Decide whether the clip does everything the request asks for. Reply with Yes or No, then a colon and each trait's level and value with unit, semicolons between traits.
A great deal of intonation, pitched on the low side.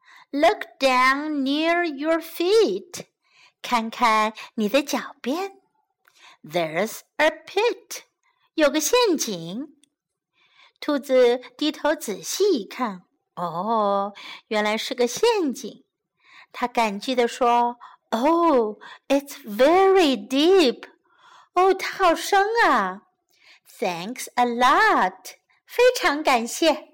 No: wide, 7.3 semitones; very high, 290 Hz